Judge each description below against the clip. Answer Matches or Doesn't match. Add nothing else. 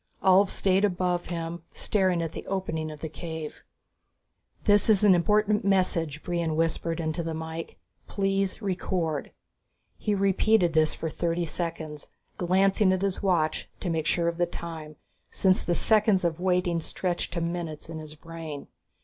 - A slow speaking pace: Doesn't match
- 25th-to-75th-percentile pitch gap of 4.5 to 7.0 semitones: Doesn't match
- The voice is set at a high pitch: Doesn't match